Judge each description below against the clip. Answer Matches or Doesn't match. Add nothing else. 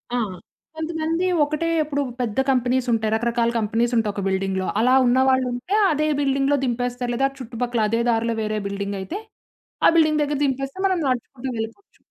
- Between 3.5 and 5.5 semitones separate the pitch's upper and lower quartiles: Matches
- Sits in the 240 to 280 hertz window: Matches